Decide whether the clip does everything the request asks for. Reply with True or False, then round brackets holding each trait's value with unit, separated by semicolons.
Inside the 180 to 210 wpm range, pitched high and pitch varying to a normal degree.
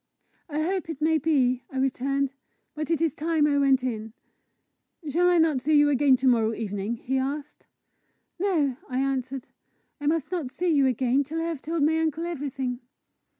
True (190 wpm; 285 Hz; 3.6 semitones)